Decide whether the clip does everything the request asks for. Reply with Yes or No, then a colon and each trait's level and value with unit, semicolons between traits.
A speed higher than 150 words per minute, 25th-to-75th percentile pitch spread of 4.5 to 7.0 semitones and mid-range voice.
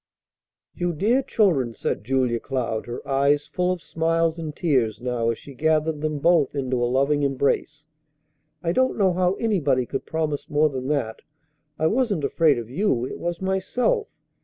Yes: average, 170 wpm; average, 4.9 semitones; medium, 150 Hz